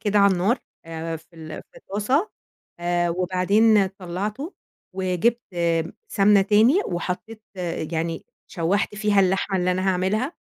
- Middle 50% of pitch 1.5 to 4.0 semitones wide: Yes, average, 3.3 semitones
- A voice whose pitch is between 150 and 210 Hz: Yes, high, 190 Hz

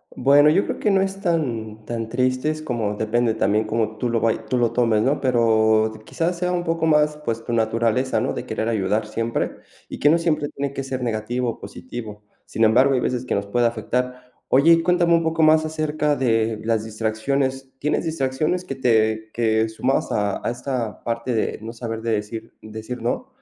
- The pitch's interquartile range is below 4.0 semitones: No, average, 4.8 semitones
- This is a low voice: Yes, low, 120 Hz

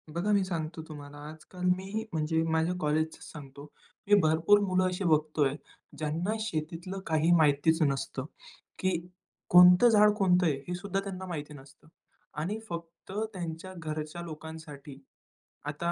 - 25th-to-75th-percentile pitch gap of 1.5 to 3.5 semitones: Yes, average, 3.2 semitones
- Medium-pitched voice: Yes, medium, 165 Hz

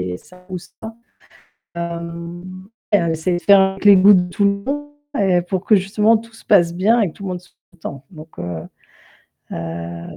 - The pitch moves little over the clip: No, average, 3.5 semitones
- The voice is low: No, medium, 185 Hz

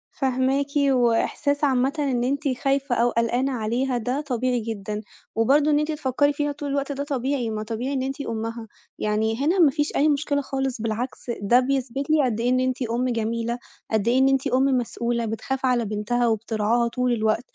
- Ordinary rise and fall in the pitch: Yes, average, 3.1 semitones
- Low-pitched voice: No, very high, 255 Hz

